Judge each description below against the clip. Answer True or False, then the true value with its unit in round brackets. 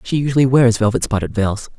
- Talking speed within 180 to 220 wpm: True (200 wpm)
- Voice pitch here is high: False (115 Hz)